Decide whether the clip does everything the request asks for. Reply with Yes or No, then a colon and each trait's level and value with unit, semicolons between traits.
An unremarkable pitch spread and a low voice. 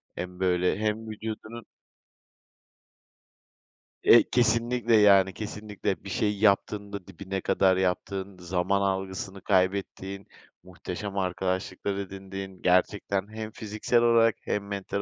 No: narrow, 2.0 semitones; low, 100 Hz